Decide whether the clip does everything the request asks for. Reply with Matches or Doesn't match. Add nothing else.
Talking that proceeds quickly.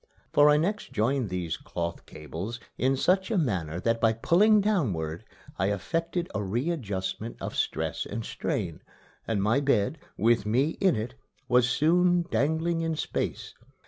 Doesn't match